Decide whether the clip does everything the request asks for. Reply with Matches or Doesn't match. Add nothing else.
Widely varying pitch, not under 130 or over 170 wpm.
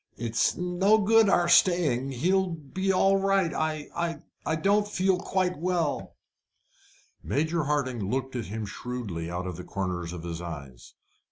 Matches